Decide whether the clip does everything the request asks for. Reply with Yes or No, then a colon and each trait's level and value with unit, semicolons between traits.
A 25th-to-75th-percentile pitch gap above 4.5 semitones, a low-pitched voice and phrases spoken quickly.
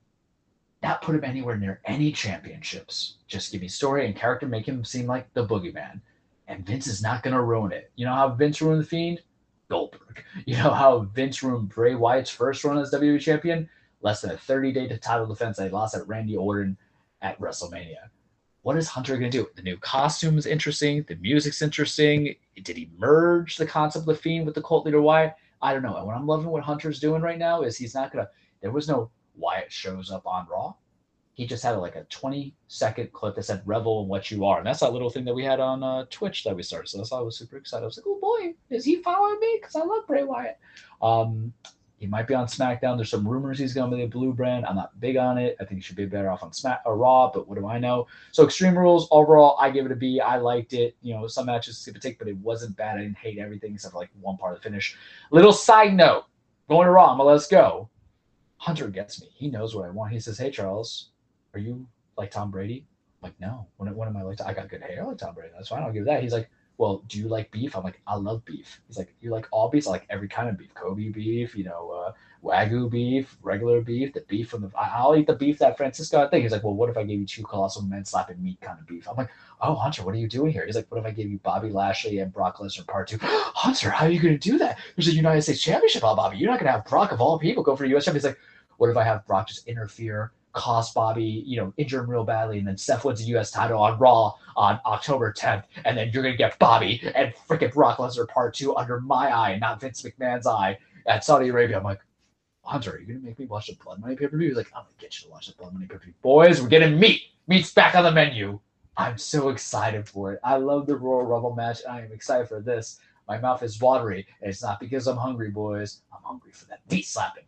Yes: wide, 5.4 semitones; low, 120 Hz; fast, 260 wpm